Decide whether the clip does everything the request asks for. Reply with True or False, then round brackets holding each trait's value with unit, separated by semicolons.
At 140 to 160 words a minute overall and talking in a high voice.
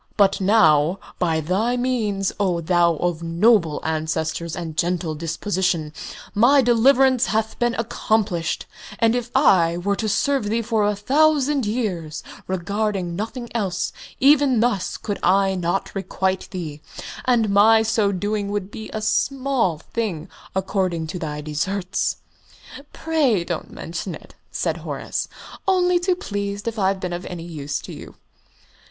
True (145 wpm; 200 Hz)